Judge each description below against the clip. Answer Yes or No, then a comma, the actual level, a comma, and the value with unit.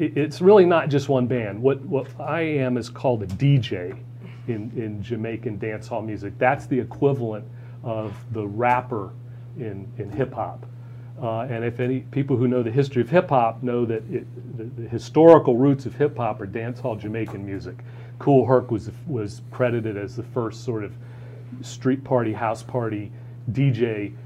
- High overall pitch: No, low, 120 Hz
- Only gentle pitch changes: Yes, narrow, 2.2 semitones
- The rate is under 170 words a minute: No, average, 175 wpm